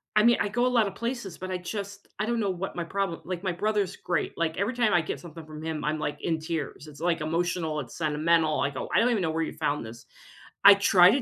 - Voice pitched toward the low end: No, medium, 175 Hz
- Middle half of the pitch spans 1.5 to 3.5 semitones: No, average, 4.3 semitones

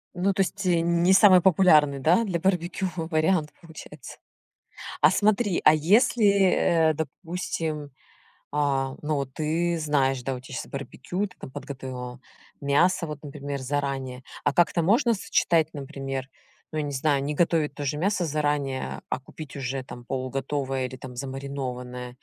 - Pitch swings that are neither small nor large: Yes, average, 4.1 semitones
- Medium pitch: Yes, medium, 150 Hz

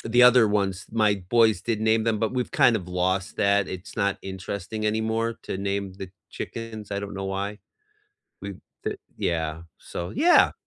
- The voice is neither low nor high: No, low, 100 Hz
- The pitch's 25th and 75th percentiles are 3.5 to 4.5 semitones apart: No, narrow, 2.5 semitones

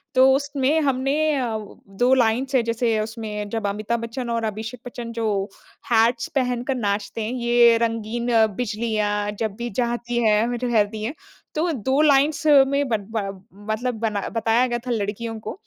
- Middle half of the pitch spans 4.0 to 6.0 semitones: No, average, 2.7 semitones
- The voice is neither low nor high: No, high, 235 Hz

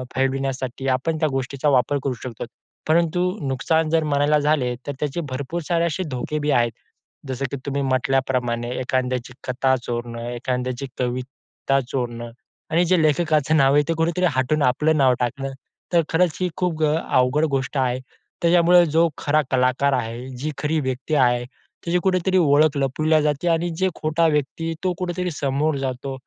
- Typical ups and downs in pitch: Yes, average, 3.7 semitones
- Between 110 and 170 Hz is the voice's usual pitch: Yes, medium, 140 Hz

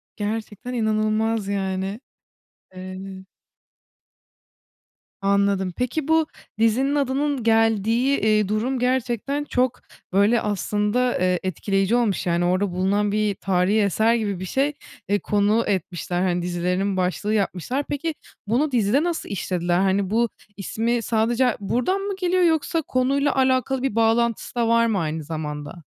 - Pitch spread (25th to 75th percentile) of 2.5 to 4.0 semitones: No, average, 4.6 semitones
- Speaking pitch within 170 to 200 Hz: No, high, 215 Hz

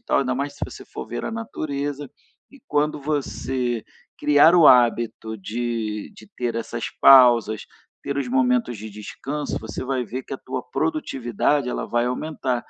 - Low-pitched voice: Yes, low, 130 Hz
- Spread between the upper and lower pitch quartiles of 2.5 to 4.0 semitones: Yes, average, 3.4 semitones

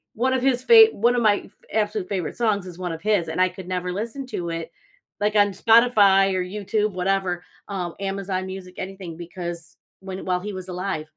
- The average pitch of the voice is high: Yes, high, 195 Hz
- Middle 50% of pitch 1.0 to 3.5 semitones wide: Yes, average, 2.7 semitones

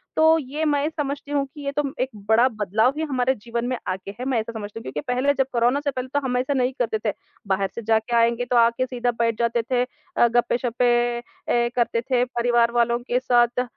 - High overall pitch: Yes, high, 245 Hz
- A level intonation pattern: Yes, narrow, 2.0 semitones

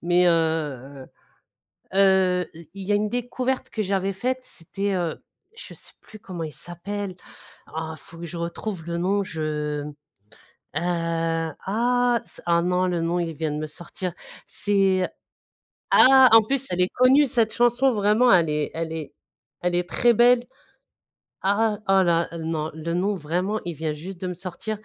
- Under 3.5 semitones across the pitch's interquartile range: No, average, 4.2 semitones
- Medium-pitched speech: Yes, medium, 180 Hz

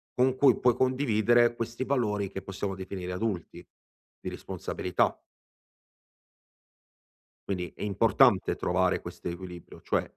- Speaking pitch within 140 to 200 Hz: No, low, 105 Hz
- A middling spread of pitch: Yes, average, 4.6 semitones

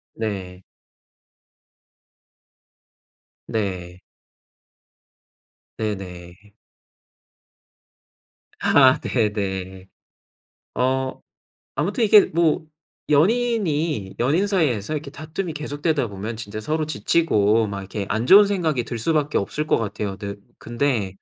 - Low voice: Yes, low, 120 Hz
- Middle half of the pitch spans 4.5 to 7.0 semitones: No, wide, 7.5 semitones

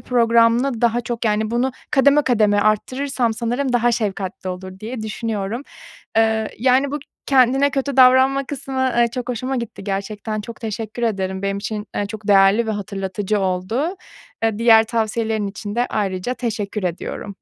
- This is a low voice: No, high, 225 Hz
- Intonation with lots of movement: No, average, 3.4 semitones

